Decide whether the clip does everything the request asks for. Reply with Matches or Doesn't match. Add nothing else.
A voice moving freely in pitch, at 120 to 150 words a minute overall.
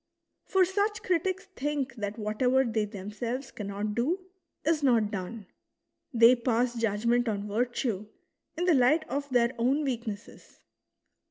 Doesn't match